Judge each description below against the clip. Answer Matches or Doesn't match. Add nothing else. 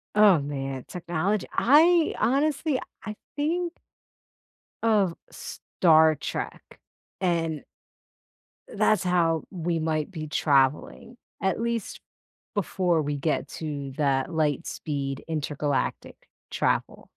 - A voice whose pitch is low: Doesn't match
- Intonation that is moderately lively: Doesn't match